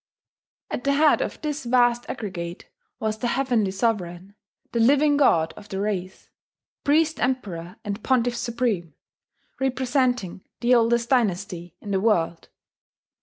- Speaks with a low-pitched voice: No, high, 230 Hz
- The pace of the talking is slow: Yes, slow, 130 wpm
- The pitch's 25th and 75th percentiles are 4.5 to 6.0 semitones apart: Yes, average, 5.0 semitones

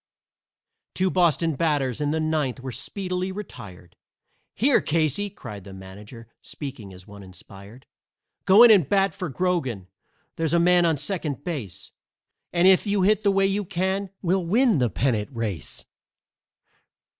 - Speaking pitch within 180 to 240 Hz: No, medium, 160 Hz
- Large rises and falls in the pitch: Yes, wide, 8.4 semitones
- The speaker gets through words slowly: No, average, 150 wpm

